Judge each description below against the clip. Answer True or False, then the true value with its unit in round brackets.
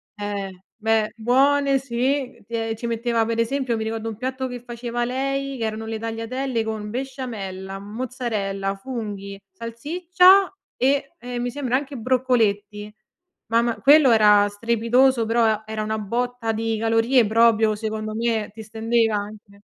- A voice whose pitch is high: True (230 Hz)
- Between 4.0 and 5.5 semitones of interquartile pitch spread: False (2.8 semitones)